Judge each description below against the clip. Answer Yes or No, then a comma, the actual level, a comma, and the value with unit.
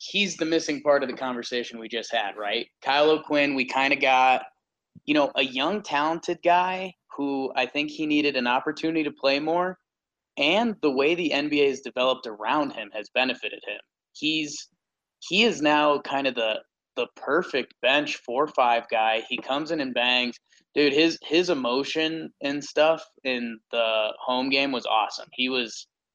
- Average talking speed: Yes, average, 175 wpm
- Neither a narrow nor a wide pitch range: Yes, average, 4.2 semitones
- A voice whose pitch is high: No, medium, 145 Hz